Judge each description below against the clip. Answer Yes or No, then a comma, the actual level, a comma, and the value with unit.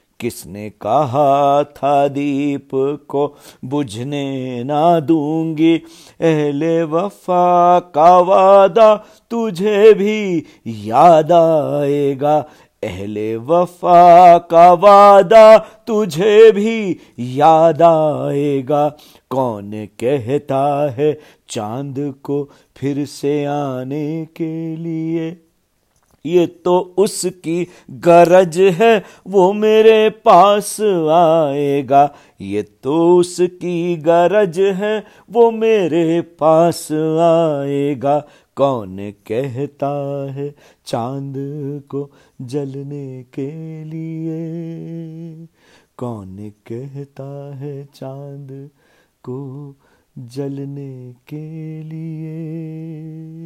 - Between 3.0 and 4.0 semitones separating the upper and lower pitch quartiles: Yes, average, 3.6 semitones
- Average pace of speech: No, slow, 75 wpm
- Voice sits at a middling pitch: Yes, medium, 155 Hz